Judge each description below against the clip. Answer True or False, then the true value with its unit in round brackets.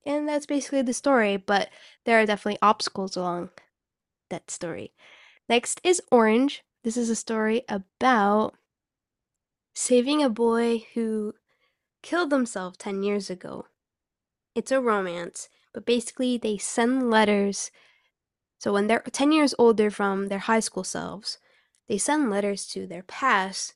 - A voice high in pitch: True (225 Hz)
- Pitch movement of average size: True (4.0 semitones)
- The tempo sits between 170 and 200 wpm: False (140 wpm)